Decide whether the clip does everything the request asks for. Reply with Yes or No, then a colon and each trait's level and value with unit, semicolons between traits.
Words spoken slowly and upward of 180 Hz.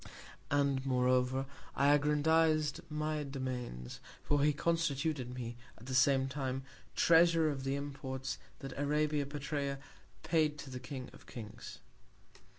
No: slow, 130 wpm; medium, 140 Hz